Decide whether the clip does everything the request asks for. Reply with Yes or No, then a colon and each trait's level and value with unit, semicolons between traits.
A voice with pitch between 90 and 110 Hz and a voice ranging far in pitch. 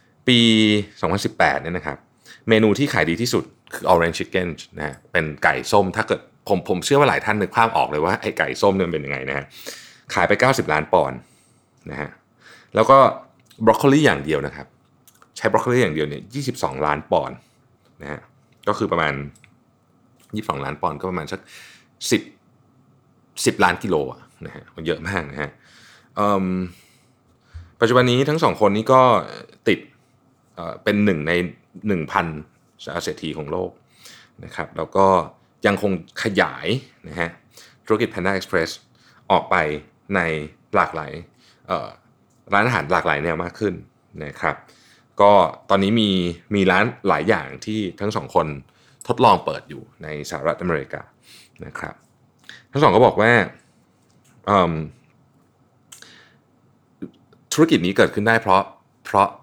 Yes: low, 100 Hz; wide, 5.7 semitones